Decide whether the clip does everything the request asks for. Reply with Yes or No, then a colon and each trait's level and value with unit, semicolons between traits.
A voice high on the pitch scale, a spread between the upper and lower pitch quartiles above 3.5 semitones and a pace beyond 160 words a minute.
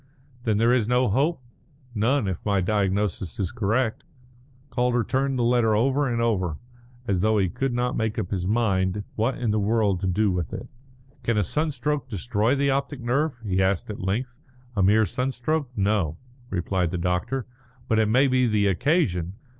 No: low, 110 Hz; average, 4.6 semitones; average, 180 wpm